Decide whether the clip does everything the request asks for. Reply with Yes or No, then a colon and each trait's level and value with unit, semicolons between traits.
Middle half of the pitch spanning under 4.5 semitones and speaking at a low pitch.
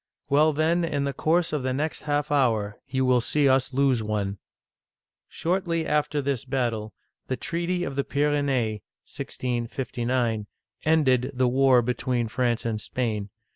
Yes: average, 3.7 semitones; low, 130 Hz